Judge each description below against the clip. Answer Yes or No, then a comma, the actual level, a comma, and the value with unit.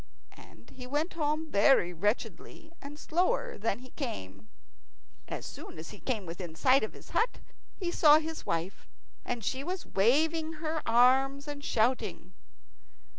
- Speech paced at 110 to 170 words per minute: Yes, average, 150 wpm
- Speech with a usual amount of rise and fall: No, wide, 6.4 semitones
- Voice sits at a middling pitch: No, very high, 270 Hz